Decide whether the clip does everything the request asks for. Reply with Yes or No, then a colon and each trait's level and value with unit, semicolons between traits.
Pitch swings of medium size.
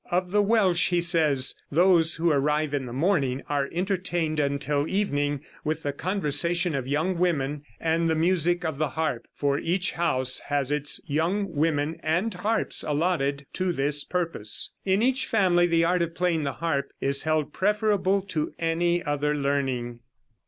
Yes: average, 3.8 semitones